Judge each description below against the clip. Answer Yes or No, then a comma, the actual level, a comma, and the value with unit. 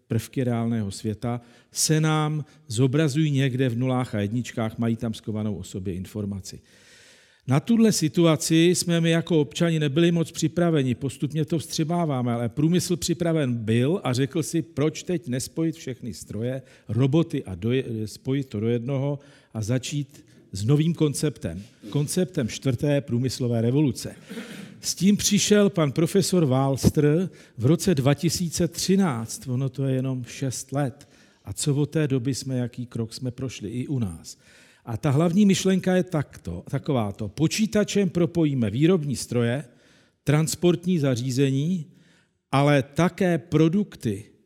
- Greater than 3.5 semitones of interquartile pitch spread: Yes, average, 5.2 semitones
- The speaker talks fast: No, average, 140 wpm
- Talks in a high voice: No, medium, 140 Hz